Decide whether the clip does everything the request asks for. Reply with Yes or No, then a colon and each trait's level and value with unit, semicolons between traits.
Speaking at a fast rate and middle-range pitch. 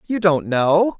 No: average, 180 wpm; medium, 175 Hz